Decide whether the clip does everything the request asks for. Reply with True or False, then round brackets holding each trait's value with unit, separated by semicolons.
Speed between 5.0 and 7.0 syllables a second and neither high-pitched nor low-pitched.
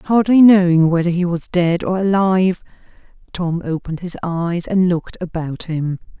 False (4.8 syllables/s; 175 Hz)